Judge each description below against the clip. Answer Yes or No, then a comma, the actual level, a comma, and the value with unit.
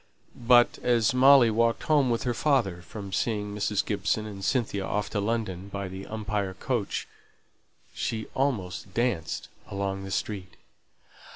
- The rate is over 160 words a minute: No, average, 145 wpm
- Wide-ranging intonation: No, average, 3.4 semitones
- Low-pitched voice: Yes, low, 105 Hz